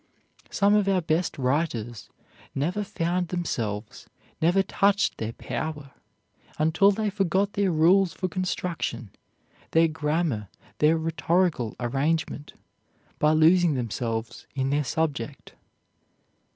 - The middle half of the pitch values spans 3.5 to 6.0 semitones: Yes, average, 5.2 semitones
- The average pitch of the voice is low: No, medium, 160 Hz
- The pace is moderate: No, slow, 110 wpm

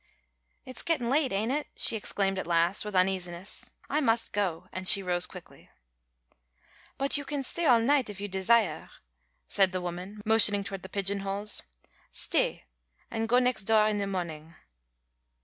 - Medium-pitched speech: No, high, 200 Hz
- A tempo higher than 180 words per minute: No, average, 165 wpm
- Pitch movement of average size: Yes, average, 3.8 semitones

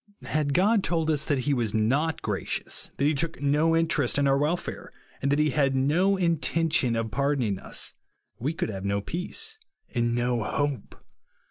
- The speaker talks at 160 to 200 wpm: Yes, average, 175 wpm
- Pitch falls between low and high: Yes, medium, 145 Hz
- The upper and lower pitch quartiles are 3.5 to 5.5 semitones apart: Yes, average, 4.9 semitones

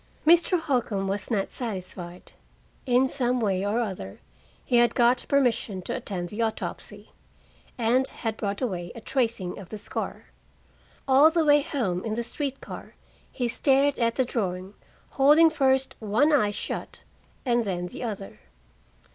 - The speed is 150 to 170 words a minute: Yes, average, 155 wpm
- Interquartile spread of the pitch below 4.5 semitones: No, average, 5.0 semitones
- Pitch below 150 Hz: No, high, 235 Hz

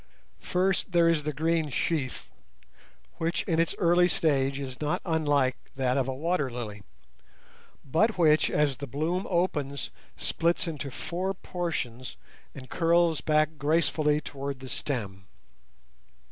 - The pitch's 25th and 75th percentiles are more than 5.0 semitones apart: No, average, 3.8 semitones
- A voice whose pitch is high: No, medium, 150 Hz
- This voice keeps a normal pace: No, slow, 130 wpm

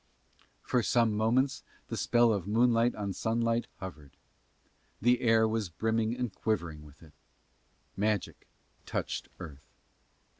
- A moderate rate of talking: No, slow, 120 wpm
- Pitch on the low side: Yes, low, 110 Hz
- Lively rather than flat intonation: No, average, 3.8 semitones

